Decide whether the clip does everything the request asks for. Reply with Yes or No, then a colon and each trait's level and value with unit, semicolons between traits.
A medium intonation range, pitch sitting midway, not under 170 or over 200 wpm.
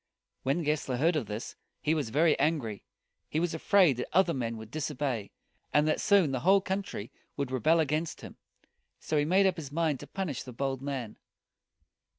Yes: average, 4.3 semitones; medium, 150 Hz; average, 185 wpm